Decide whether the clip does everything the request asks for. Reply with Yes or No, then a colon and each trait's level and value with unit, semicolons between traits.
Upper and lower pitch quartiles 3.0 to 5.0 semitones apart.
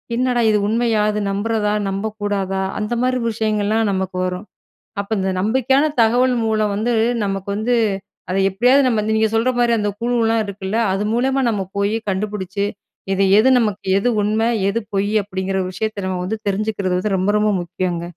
No: narrow, 2.5 semitones